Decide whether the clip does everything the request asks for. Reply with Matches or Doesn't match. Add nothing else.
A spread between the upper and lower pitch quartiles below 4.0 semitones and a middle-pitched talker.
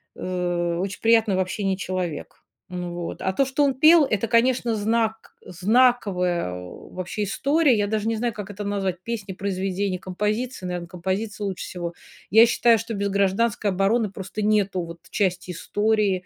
Doesn't match